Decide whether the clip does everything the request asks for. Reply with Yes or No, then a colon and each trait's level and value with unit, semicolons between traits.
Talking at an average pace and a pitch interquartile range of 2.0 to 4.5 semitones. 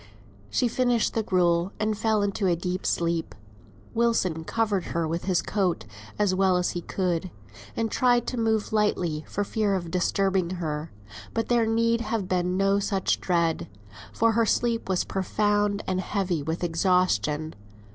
Yes: average, 160 wpm; average, 3.9 semitones